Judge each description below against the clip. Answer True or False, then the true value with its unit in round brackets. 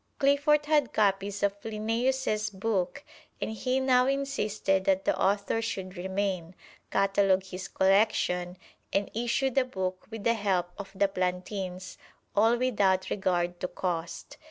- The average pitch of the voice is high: True (200 Hz)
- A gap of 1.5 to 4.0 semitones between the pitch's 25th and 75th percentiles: True (3.6 semitones)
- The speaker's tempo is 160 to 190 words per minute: False (135 wpm)